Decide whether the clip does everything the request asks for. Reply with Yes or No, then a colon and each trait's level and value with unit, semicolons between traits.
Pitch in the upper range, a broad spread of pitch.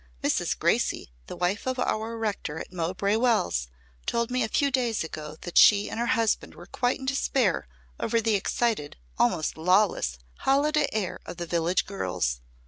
Yes: high, 210 Hz; wide, 5.8 semitones